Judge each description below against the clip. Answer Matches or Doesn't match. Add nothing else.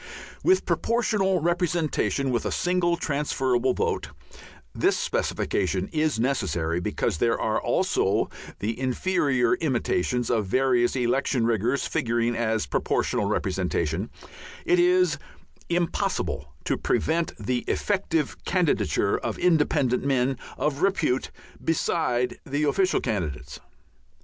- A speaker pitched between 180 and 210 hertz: Doesn't match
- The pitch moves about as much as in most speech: Doesn't match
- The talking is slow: Matches